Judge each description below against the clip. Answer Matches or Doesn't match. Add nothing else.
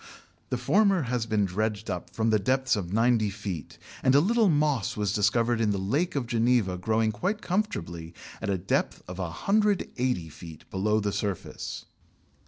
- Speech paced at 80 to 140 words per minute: Doesn't match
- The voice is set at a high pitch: Doesn't match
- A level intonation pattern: Doesn't match